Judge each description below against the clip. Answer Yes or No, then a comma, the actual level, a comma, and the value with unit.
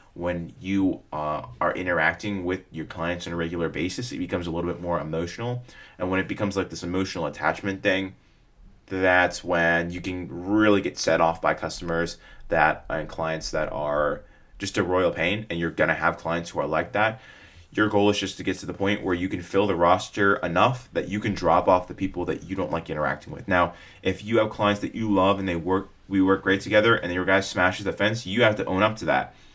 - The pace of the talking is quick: Yes, fast, 230 wpm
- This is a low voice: Yes, very low, 95 Hz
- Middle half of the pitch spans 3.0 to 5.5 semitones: No, narrow, 2.6 semitones